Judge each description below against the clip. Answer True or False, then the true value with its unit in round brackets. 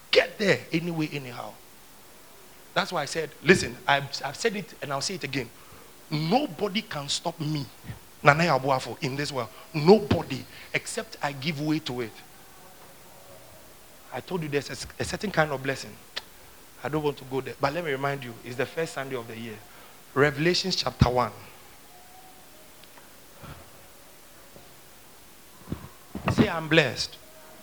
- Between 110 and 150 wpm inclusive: True (140 wpm)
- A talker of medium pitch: True (145 Hz)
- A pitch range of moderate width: True (4.2 semitones)